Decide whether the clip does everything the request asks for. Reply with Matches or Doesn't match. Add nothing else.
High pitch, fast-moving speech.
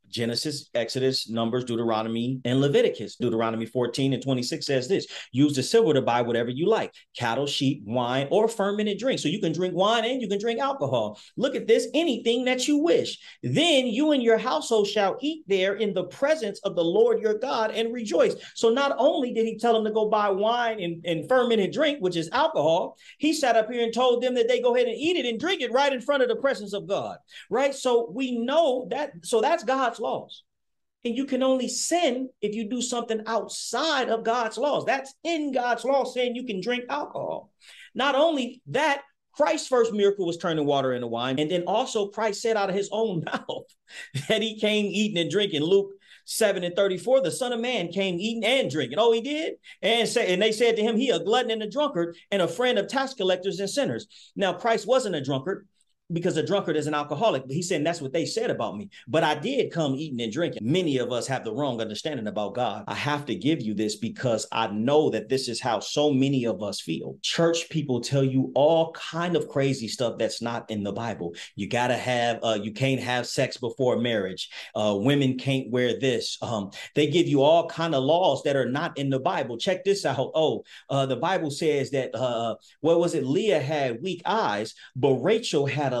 Matches